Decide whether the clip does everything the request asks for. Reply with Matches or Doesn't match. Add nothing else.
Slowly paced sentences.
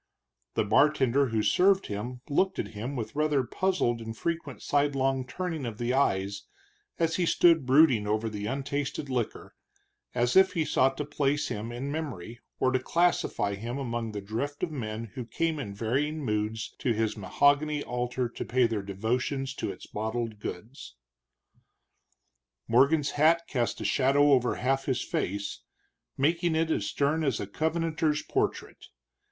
Doesn't match